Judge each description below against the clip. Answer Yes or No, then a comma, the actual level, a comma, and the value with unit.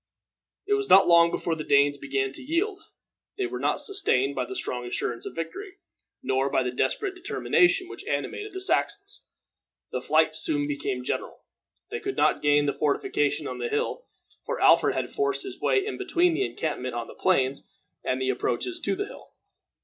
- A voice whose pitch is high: Yes, very high, 305 Hz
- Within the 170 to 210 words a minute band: Yes, average, 190 wpm